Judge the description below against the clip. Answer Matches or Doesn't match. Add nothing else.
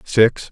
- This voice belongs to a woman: Doesn't match